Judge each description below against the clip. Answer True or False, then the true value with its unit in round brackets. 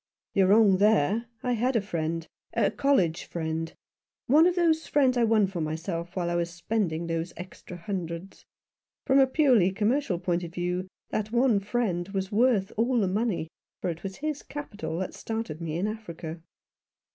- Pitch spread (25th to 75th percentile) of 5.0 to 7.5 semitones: True (5.3 semitones)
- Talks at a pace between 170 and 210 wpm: True (180 wpm)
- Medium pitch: False (195 Hz)